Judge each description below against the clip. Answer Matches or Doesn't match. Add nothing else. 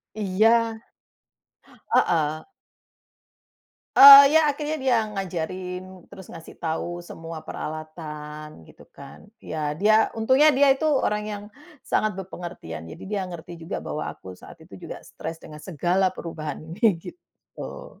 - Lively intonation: Matches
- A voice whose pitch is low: Doesn't match